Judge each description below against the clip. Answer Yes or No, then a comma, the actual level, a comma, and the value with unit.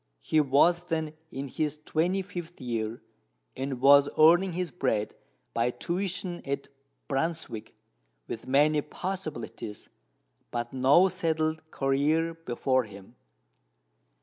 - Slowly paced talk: Yes, slow, 110 wpm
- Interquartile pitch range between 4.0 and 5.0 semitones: Yes, average, 4.3 semitones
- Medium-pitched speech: Yes, medium, 150 Hz